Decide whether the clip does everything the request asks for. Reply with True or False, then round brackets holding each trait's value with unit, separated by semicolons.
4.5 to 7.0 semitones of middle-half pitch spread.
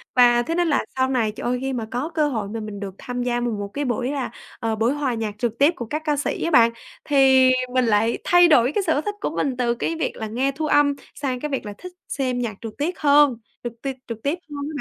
False (3.8 semitones)